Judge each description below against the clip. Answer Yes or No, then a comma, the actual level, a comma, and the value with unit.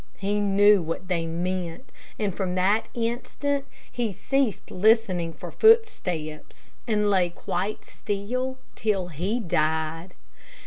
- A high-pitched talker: Yes, high, 195 Hz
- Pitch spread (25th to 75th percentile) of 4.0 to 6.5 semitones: Yes, average, 4.3 semitones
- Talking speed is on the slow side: Yes, slow, 120 wpm